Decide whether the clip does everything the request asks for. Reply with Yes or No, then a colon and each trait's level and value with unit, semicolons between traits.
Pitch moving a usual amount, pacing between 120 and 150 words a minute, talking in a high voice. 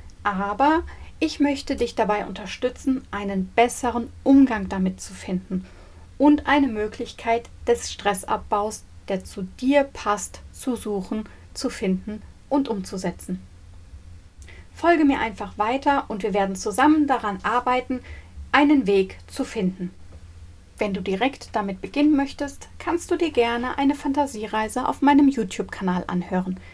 No: wide, 6.0 semitones; average, 130 wpm; high, 220 Hz